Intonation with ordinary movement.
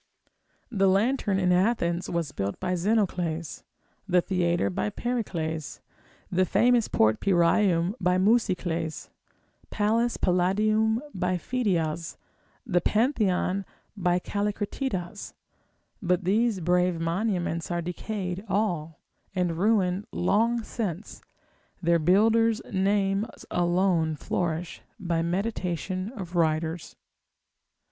Yes: average, 3.5 semitones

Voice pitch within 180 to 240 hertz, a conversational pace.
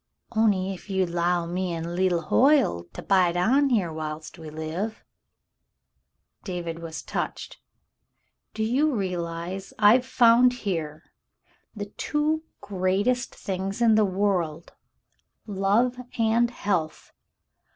No: high, 190 Hz; slow, 120 wpm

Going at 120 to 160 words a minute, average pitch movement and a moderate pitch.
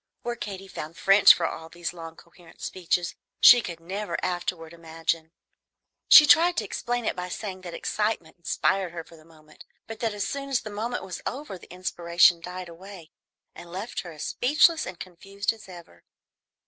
No: average, 185 wpm; average, 3.8 semitones; medium, 180 Hz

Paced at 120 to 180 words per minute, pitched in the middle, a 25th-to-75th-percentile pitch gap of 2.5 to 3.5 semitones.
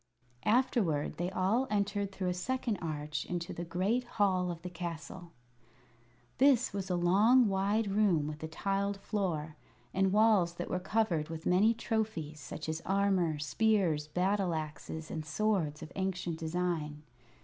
No: average, 150 wpm; medium, 180 Hz; average, 4.1 semitones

